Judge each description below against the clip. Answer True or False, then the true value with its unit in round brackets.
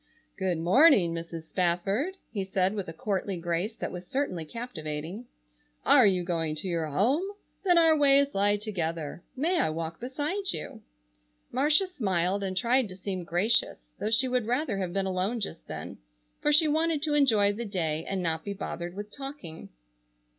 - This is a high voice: True (200 Hz)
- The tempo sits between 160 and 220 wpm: True (175 wpm)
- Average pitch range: False (7.1 semitones)